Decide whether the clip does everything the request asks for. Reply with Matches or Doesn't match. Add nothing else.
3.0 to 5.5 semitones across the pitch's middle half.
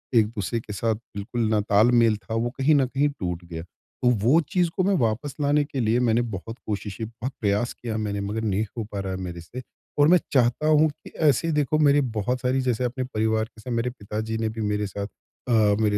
Matches